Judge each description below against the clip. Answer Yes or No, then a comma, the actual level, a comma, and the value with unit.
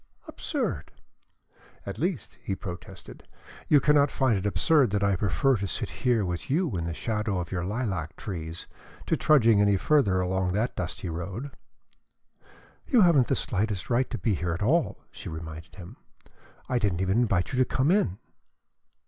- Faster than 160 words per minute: Yes, average, 170 wpm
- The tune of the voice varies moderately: No, wide, 6.0 semitones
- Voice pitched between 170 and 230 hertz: No, low, 100 Hz